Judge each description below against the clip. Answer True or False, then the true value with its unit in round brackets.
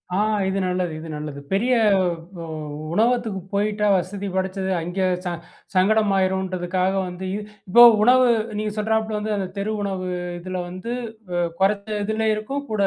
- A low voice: False (195 Hz)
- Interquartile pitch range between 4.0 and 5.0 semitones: False (2.7 semitones)